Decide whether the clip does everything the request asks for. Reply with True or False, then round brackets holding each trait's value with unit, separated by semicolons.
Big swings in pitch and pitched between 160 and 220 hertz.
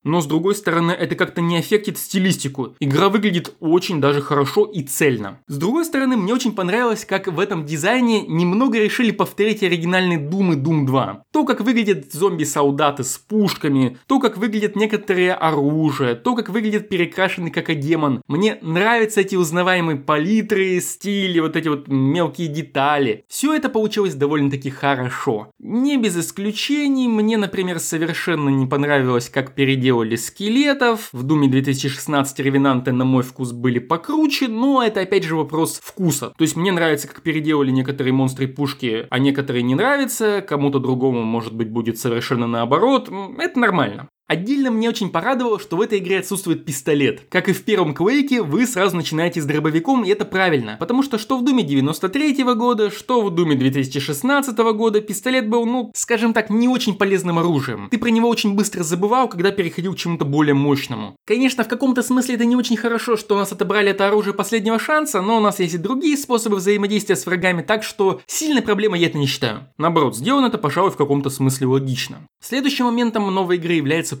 True (7.3 semitones; 185 Hz)